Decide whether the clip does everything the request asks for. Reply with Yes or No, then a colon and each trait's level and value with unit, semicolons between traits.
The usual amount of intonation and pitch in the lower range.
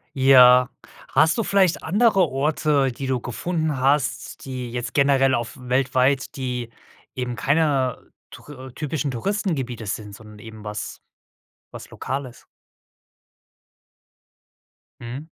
Yes: average, 3.1 semitones; low, 130 Hz